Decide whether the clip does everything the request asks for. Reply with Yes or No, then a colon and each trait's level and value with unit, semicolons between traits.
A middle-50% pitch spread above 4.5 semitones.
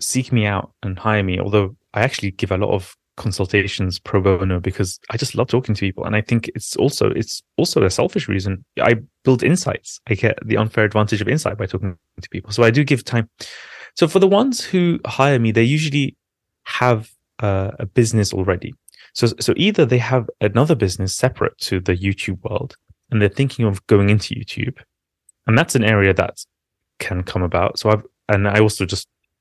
No: average, 4.2 semitones